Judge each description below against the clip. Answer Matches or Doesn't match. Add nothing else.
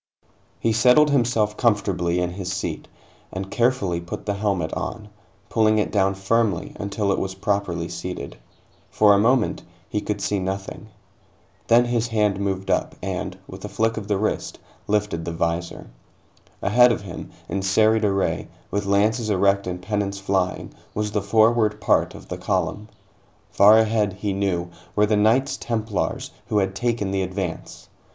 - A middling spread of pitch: Doesn't match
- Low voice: Matches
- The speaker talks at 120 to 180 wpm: Matches